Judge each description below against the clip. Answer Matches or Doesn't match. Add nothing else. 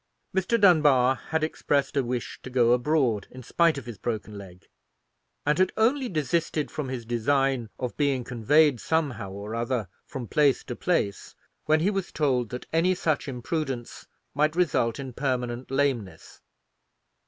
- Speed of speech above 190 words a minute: Doesn't match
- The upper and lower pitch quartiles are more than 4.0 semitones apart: Matches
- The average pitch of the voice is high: Doesn't match